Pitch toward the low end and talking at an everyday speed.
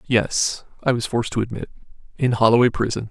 Yes: low, 115 Hz; average, 175 wpm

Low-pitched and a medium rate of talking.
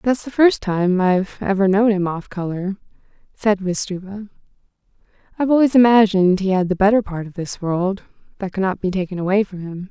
No: high, 195 Hz; average, 190 wpm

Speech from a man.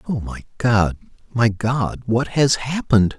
Yes: male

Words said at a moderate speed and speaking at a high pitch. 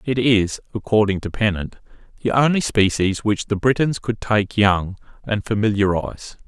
No: average, 150 wpm; low, 105 Hz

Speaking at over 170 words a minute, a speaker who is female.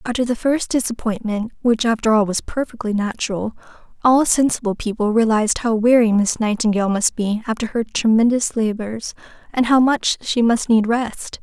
No: average, 150 wpm; female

